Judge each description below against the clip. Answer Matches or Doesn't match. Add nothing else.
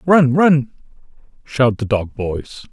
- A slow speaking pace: Matches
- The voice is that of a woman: Doesn't match